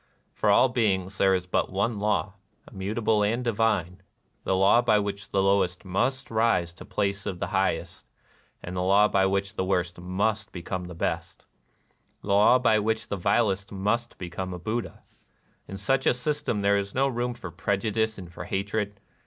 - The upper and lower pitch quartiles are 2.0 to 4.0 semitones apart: Yes, average, 2.7 semitones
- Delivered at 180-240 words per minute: Yes, average, 190 wpm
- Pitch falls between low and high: No, low, 100 Hz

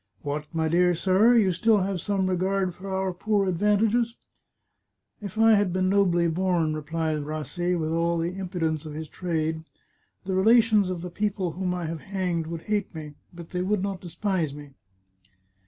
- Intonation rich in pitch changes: No, average, 3.2 semitones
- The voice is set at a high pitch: No, medium, 180 Hz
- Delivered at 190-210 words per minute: Yes, average, 195 wpm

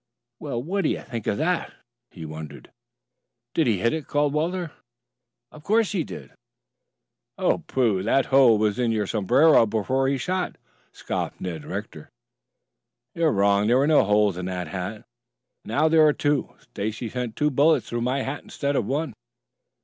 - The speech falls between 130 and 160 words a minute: No, average, 170 wpm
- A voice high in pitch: No, low, 130 Hz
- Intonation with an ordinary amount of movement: No, wide, 6.5 semitones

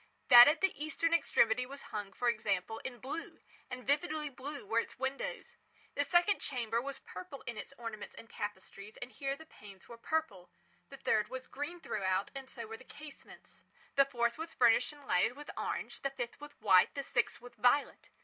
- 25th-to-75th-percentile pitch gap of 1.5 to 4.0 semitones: No, average, 4.4 semitones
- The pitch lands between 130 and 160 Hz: No, very high, 250 Hz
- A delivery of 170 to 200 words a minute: Yes, average, 185 wpm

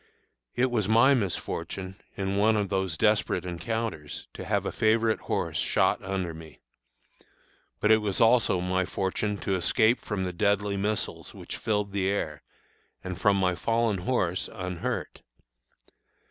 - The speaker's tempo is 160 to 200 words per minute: No, average, 145 wpm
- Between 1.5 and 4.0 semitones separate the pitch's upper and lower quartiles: Yes, average, 3.0 semitones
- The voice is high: No, low, 100 Hz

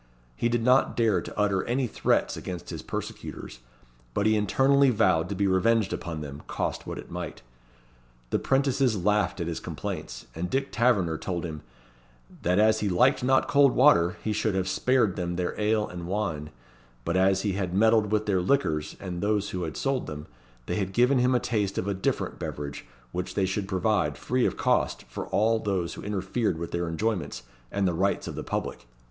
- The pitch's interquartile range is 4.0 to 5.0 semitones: Yes, average, 4.3 semitones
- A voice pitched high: No, low, 100 Hz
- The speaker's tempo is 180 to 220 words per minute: Yes, average, 200 wpm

